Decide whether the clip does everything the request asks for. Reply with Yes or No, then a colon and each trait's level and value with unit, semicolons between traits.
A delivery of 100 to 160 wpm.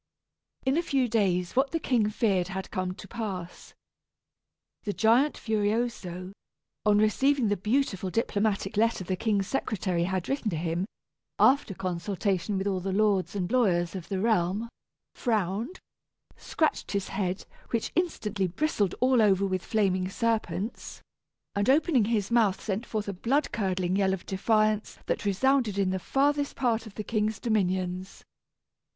Yes: average, 150 wpm